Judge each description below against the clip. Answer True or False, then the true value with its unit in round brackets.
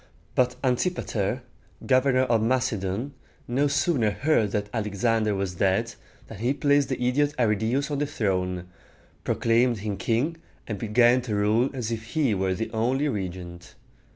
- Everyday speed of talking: True (155 wpm)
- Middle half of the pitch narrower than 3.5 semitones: False (4.0 semitones)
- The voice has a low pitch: True (115 Hz)